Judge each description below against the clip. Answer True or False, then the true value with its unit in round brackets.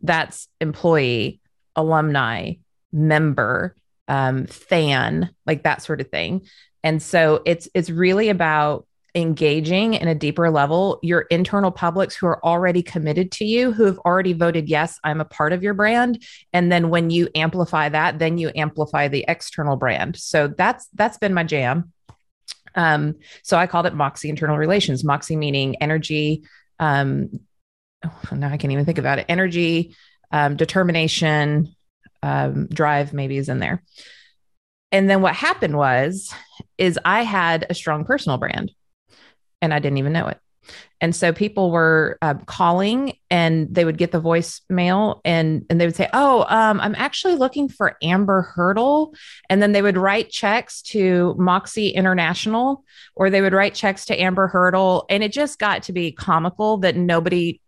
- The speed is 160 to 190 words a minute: True (165 wpm)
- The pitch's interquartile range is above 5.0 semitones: False (3.8 semitones)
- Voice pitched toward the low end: False (170 Hz)